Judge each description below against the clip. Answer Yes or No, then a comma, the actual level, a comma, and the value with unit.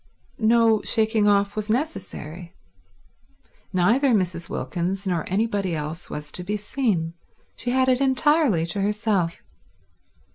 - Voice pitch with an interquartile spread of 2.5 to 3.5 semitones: No, average, 4.8 semitones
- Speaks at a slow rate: Yes, slow, 120 wpm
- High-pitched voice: Yes, high, 205 Hz